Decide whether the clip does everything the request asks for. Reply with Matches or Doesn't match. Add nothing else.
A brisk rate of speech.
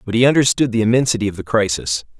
Matches